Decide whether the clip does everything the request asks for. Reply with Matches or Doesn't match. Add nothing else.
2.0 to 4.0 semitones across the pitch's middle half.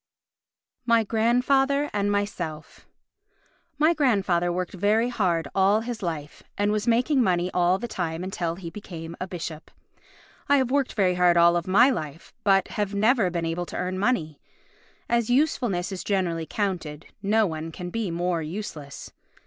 Doesn't match